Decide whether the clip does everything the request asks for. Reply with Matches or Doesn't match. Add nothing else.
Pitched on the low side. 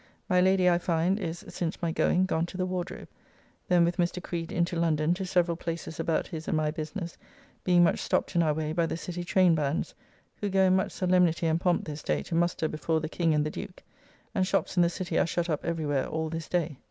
Doesn't match